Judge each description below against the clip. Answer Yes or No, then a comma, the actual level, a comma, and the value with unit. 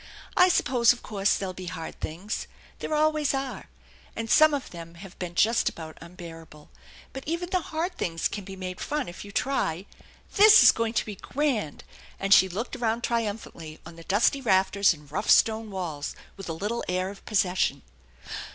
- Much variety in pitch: Yes, wide, 6.2 semitones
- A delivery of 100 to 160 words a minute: No, average, 190 wpm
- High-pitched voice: Yes, high, 200 Hz